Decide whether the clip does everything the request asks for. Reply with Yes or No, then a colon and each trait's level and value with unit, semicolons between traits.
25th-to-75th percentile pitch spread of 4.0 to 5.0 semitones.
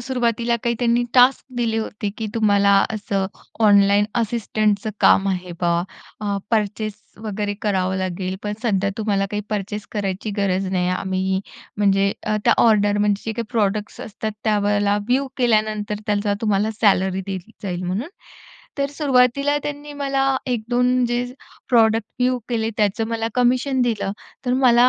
No: average, 3.1 semitones